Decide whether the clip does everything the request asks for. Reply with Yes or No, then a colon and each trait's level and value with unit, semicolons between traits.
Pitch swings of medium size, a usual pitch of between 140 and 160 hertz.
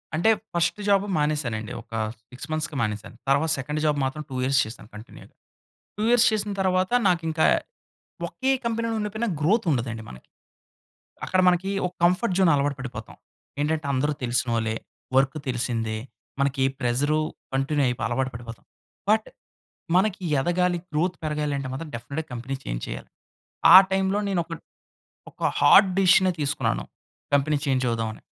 No: wide, 6.5 semitones; medium, 150 Hz